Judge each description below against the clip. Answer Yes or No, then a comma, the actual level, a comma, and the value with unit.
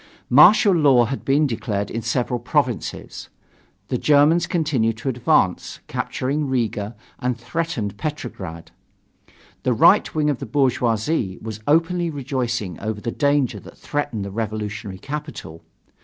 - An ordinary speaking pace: No, slow, 130 wpm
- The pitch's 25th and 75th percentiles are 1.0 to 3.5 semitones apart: No, average, 5.3 semitones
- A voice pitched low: Yes, low, 125 Hz